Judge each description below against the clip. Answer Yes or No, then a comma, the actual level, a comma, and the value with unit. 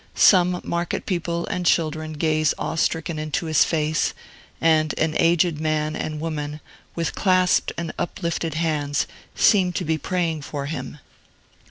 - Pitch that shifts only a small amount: Yes, narrow, 1.8 semitones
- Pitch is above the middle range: No, medium, 160 Hz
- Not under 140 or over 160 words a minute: Yes, average, 145 wpm